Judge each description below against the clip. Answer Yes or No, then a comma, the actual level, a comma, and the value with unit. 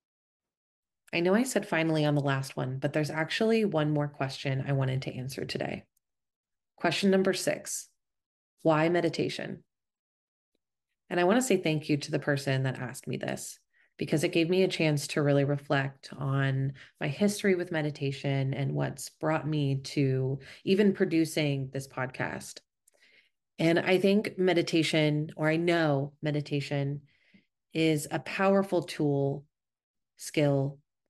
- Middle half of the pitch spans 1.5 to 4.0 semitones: Yes, average, 3.6 semitones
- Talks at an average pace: Yes, average, 145 wpm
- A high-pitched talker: No, medium, 150 Hz